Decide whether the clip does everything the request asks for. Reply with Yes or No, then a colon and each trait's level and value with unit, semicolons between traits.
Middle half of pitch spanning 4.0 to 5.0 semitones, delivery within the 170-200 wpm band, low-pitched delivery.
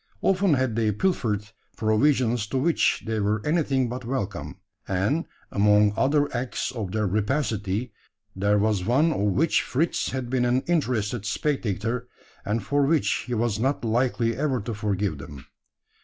No: average, 4.3 semitones; average, 155 wpm; low, 115 Hz